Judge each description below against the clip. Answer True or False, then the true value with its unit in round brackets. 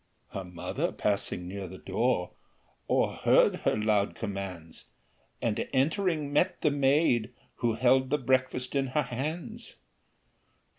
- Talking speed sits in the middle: False (120 wpm)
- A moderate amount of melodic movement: False (6.1 semitones)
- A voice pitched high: False (125 Hz)